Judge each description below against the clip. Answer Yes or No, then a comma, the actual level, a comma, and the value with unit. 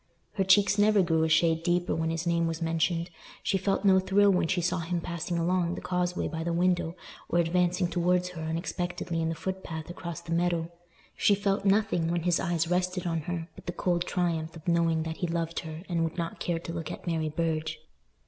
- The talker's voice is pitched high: No, medium, 170 Hz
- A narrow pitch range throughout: Yes, narrow, 1.6 semitones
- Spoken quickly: Yes, fast, 215 wpm